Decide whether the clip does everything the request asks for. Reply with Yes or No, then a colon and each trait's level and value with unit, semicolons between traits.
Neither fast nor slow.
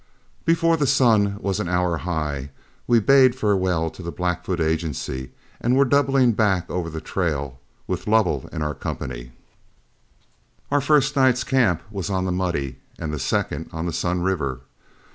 Yes: average, 160 wpm